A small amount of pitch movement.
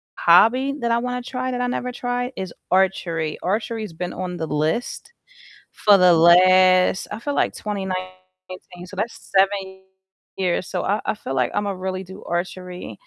No: average, 3.2 semitones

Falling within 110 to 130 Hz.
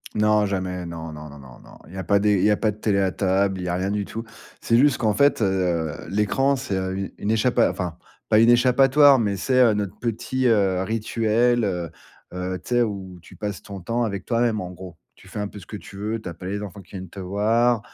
No: low, 100 Hz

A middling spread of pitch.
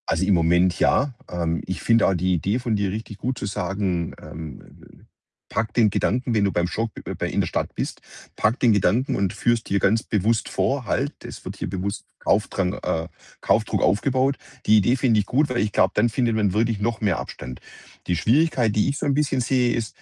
Yes: average, 4.2 semitones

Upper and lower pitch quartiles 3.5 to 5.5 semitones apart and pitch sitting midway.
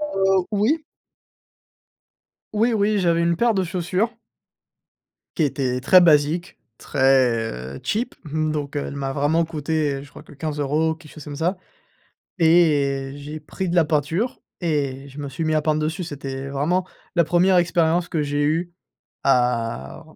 Yes: average, 3.8 semitones; medium, 155 Hz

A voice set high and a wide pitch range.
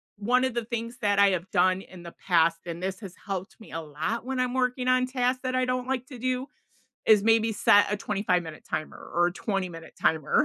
Yes: high, 210 Hz; wide, 5.9 semitones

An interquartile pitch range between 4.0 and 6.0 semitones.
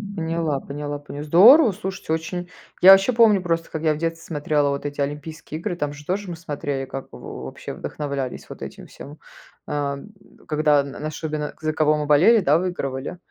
No: average, 2.9 semitones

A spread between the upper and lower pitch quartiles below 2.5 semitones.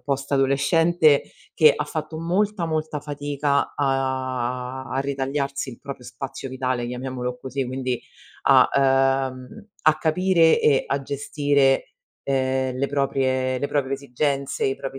Yes: narrow, 1.9 semitones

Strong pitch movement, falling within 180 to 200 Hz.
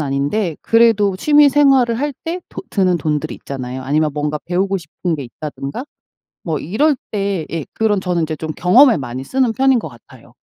Yes: wide, 7.6 semitones; medium, 185 Hz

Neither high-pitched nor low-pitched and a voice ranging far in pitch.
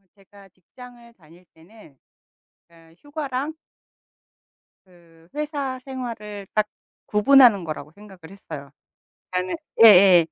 No: high, 200 Hz; wide, 6.3 semitones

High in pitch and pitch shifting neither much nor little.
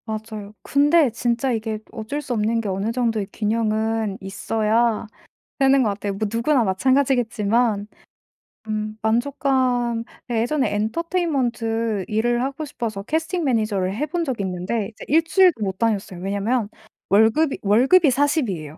Yes: high, 230 Hz; average, 4.0 semitones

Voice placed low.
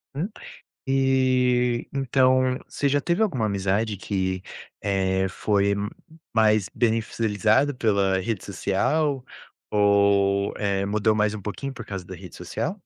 Yes: low, 105 Hz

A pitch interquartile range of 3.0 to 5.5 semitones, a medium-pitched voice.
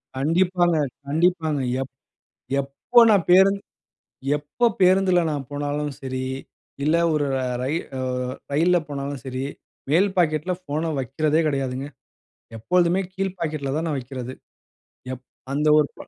Yes: average, 4.4 semitones; medium, 150 Hz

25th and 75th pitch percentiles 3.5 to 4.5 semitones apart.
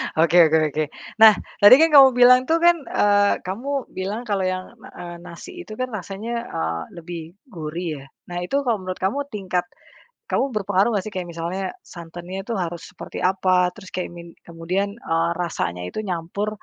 Yes: average, 3.9 semitones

